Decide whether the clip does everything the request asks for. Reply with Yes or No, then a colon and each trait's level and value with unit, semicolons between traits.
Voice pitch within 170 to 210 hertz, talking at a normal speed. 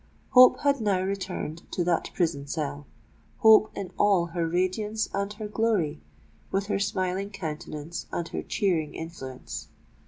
No: medium, 185 Hz; slow, 130 wpm